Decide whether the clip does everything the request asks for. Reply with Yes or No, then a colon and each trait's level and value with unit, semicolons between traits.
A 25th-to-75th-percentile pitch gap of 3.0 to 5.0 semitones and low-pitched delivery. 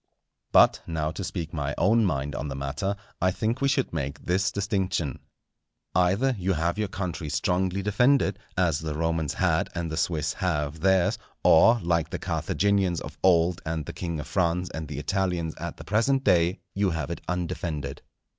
Yes: average, 3.5 semitones; very low, 85 Hz